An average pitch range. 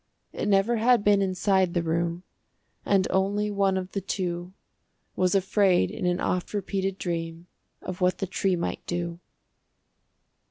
No: narrow, 2.1 semitones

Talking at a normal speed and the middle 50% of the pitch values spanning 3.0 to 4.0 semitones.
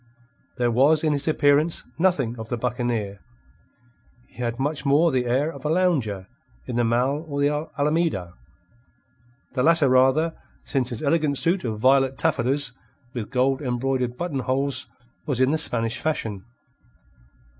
Yes: average, 150 wpm; average, 3.7 semitones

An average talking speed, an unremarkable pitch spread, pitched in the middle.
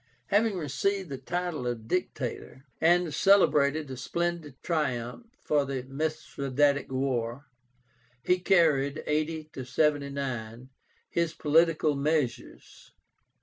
No: slow, 100 wpm; average, 3.8 semitones; medium, 150 Hz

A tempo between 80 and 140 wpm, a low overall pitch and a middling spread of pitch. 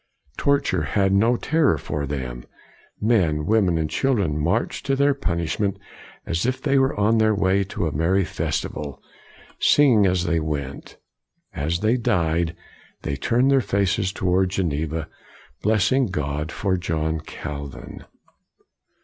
No: slow, 135 wpm; very low, 95 Hz; wide, 5.9 semitones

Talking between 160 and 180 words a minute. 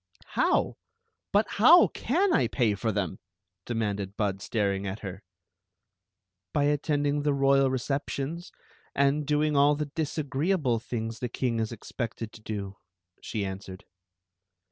No: average, 140 wpm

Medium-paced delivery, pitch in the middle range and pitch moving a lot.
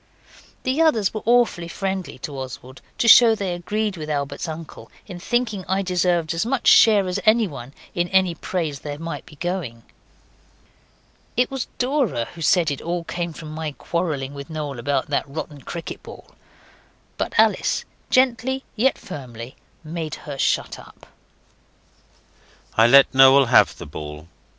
Yes: average, 155 wpm; medium, 170 Hz; wide, 6.3 semitones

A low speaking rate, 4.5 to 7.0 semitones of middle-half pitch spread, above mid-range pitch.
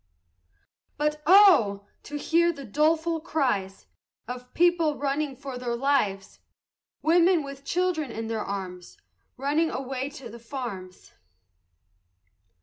Yes: slow, 115 wpm; average, 5.3 semitones; very high, 275 Hz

